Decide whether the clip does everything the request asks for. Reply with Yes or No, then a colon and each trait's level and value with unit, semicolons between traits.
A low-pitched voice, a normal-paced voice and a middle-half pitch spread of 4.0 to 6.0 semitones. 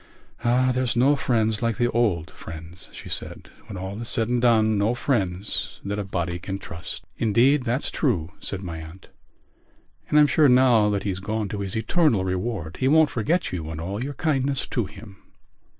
Yes: low, 110 Hz; average, 190 wpm; average, 4.9 semitones